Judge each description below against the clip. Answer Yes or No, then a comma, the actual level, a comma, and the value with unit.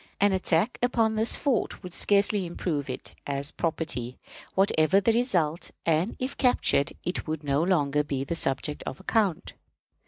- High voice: No, medium, 170 Hz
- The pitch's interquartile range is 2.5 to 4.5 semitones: No, wide, 5.6 semitones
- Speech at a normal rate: Yes, average, 155 wpm